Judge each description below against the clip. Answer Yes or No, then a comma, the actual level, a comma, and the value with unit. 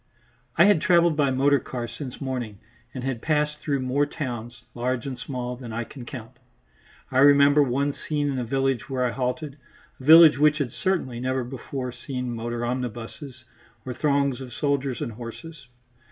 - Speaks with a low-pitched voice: Yes, low, 130 Hz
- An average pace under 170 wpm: No, average, 175 wpm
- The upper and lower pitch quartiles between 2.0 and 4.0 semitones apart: Yes, average, 2.7 semitones